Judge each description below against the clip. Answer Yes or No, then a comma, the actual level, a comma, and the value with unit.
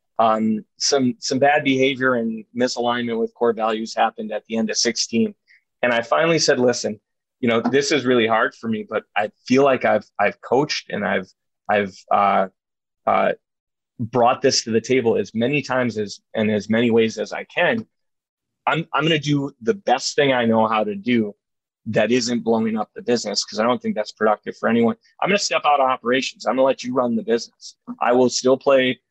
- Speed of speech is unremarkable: No, fast, 210 wpm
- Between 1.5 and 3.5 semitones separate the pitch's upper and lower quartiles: Yes, average, 2.9 semitones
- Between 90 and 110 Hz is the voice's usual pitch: No, low, 120 Hz